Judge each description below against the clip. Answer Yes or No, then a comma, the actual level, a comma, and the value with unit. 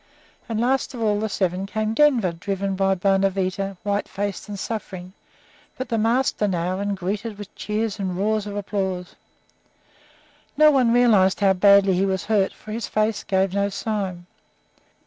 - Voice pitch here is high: Yes, high, 200 Hz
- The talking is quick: No, average, 160 wpm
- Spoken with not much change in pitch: Yes, narrow, 2.3 semitones